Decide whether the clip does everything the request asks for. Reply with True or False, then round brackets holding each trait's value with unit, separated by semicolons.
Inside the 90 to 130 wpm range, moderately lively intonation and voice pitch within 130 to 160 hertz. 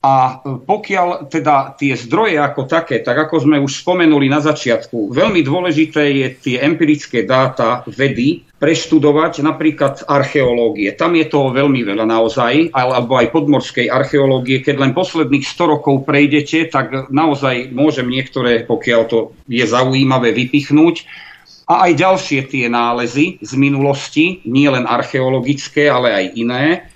False (140 wpm; 3.2 semitones; 140 Hz)